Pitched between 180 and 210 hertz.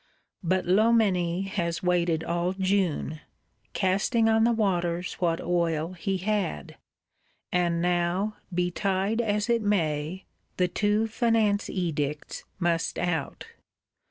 Yes: medium, 185 Hz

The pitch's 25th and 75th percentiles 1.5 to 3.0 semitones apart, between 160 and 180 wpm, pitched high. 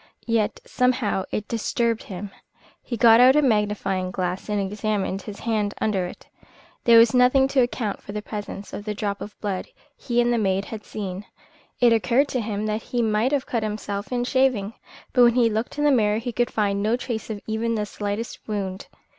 No: average, 2.7 semitones; fast, 205 wpm; high, 215 Hz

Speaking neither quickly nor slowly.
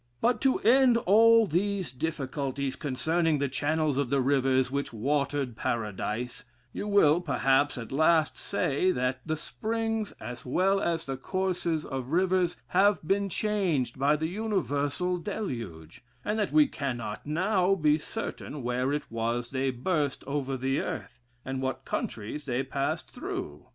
Yes: average, 150 wpm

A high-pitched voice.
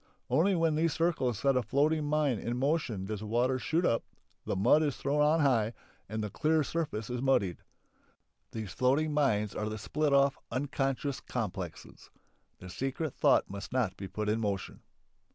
No: low, 130 Hz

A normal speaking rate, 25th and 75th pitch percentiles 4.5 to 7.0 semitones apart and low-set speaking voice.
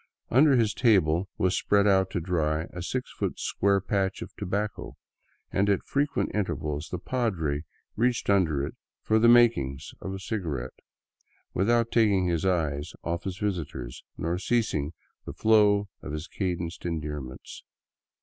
Yes: average, 155 wpm; average, 4.8 semitones; very low, 95 Hz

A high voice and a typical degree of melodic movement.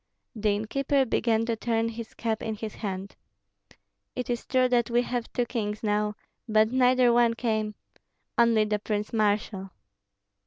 No: high, 225 Hz; narrow, 2.2 semitones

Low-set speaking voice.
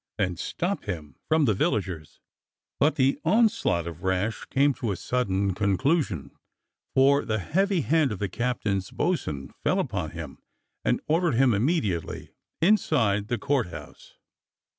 Yes: low, 115 Hz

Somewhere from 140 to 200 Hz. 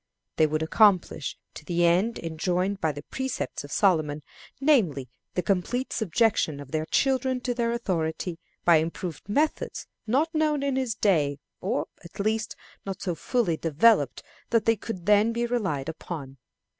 Yes: high, 190 Hz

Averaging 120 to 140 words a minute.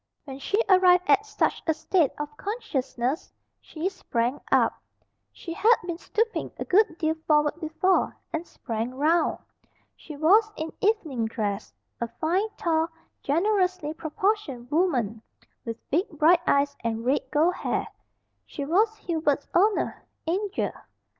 Yes: slow, 135 wpm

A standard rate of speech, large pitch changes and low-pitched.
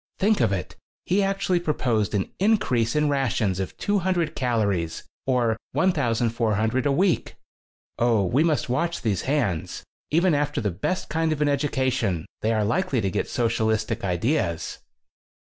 Yes: average, 145 wpm; wide, 6.4 semitones; low, 125 Hz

